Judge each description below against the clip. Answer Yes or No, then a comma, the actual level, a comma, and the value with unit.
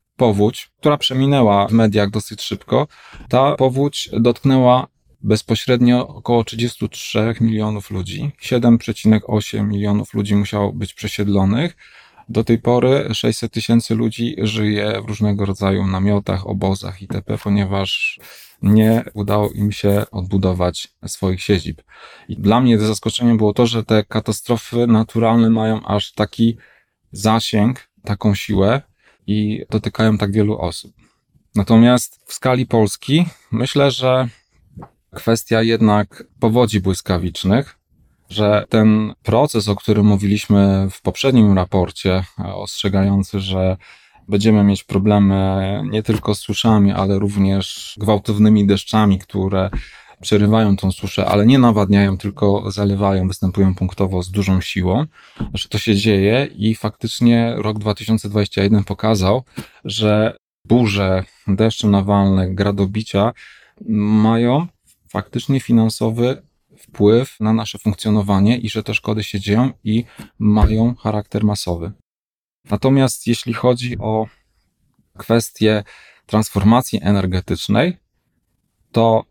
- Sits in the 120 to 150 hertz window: No, low, 105 Hz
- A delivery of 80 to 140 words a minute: Yes, slow, 110 wpm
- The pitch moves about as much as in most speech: No, narrow, 2.3 semitones